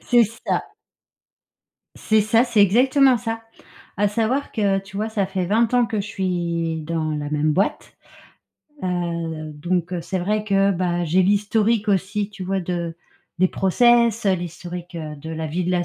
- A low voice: No, high, 190 Hz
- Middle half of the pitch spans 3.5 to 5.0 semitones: Yes, average, 3.8 semitones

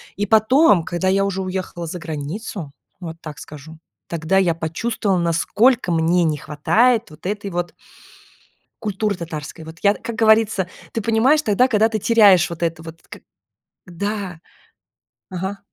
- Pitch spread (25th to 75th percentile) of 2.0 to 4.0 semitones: No, average, 4.6 semitones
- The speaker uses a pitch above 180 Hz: Yes, high, 190 Hz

